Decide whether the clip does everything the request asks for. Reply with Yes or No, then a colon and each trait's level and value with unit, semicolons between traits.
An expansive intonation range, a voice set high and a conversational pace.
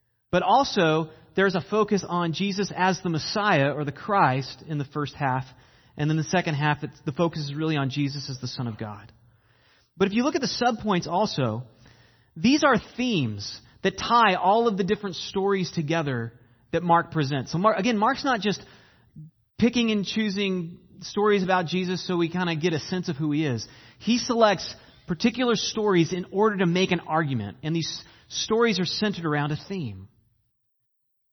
No: wide, 6.9 semitones; medium, 165 Hz; average, 185 wpm